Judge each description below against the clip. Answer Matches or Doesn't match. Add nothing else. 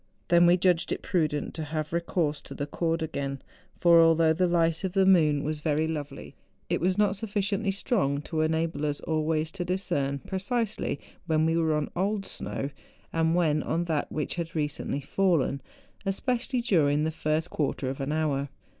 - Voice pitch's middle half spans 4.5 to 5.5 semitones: Doesn't match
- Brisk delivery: Doesn't match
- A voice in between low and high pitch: Matches